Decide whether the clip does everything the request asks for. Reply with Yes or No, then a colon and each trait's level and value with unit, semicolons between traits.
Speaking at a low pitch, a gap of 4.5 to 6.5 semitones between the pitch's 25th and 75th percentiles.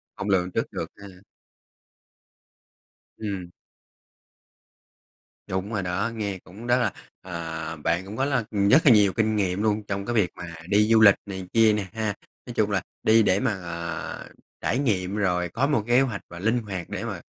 No: low, 100 Hz; average, 3.3 semitones